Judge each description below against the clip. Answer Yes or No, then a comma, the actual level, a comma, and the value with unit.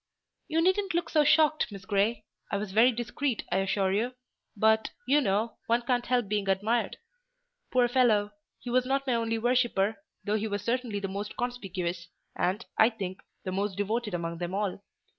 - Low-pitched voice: No, high, 220 Hz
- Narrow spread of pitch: No, average, 3.8 semitones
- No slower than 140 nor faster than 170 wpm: No, average, 180 wpm